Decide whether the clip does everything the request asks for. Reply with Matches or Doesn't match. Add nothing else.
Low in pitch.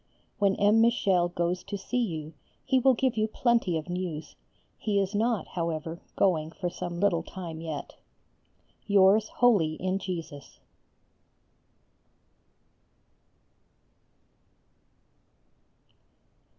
Doesn't match